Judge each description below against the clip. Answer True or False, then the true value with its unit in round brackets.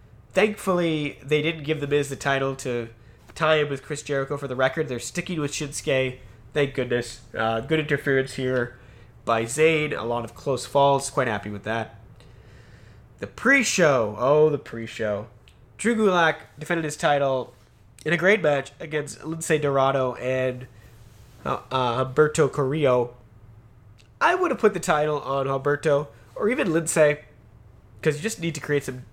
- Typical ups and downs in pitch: True (4.5 semitones)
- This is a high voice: False (135 Hz)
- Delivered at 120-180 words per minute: True (165 wpm)